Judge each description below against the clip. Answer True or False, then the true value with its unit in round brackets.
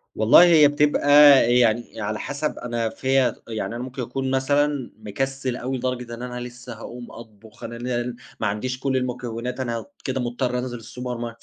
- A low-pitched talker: True (125 Hz)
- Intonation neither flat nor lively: False (2.0 semitones)